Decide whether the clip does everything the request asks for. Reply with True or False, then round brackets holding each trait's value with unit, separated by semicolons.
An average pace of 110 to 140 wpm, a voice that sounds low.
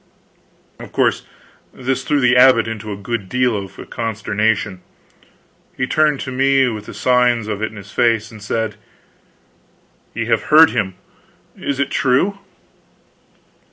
False (150 wpm; 115 Hz)